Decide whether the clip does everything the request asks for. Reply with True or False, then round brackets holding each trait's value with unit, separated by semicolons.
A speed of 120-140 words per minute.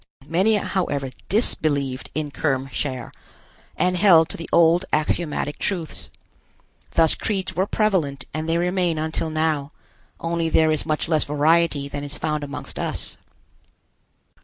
True (135 wpm)